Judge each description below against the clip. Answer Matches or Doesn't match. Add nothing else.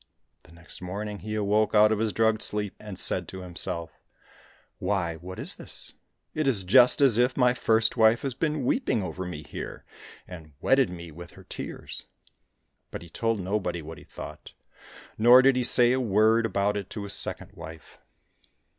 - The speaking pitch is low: Matches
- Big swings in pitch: Doesn't match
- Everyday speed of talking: Matches